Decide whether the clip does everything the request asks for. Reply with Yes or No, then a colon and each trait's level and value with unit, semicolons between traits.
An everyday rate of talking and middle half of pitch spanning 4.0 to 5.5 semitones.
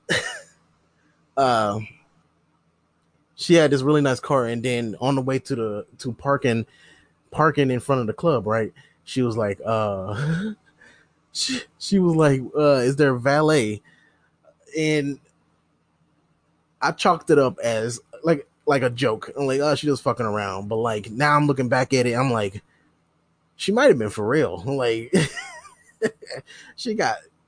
Yes: average, 160 wpm; average, 4.6 semitones